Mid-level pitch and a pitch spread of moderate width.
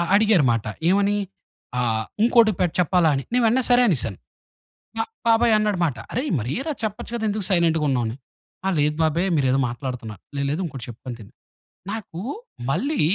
No: medium, 170 Hz; wide, 8.8 semitones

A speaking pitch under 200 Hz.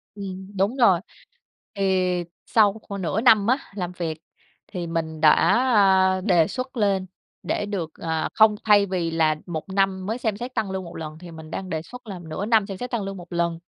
Yes: high, 190 Hz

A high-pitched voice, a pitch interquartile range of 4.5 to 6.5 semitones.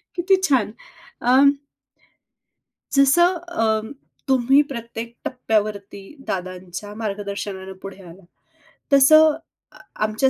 Yes: high, 225 Hz; average, 5.3 semitones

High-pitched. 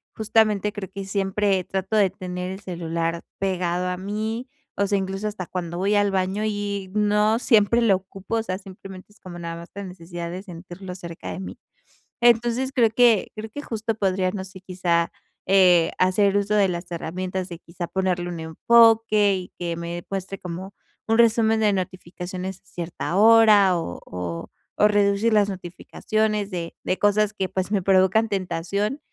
Yes: high, 195 Hz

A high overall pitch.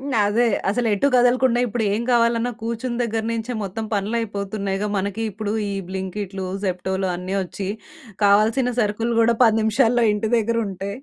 Yes: high, 220 Hz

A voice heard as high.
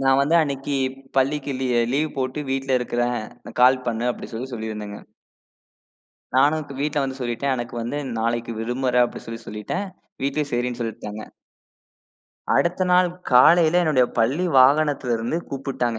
No: low, 130 Hz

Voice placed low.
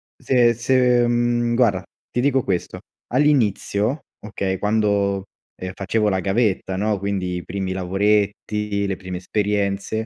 Yes: low, 105 Hz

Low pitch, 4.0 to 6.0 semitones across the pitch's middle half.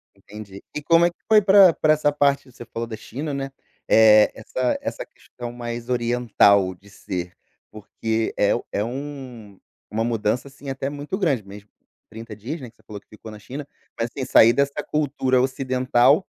Yes: low, 120 Hz; average, 4.5 semitones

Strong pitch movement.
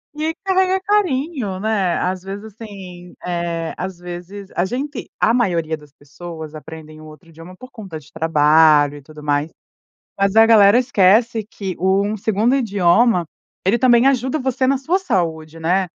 Yes: wide, 6.4 semitones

